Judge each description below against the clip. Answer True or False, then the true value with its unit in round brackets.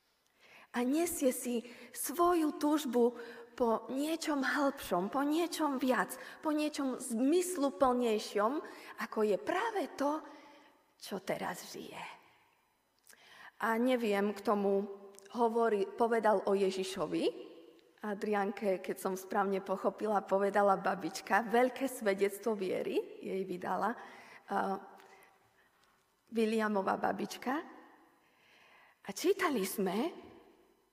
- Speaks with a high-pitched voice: True (240 Hz)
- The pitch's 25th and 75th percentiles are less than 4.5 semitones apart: False (6.9 semitones)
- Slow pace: True (90 wpm)